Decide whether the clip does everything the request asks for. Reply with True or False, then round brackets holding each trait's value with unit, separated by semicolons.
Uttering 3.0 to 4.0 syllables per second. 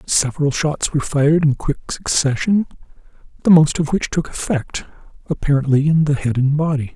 False (5.4 syllables/s)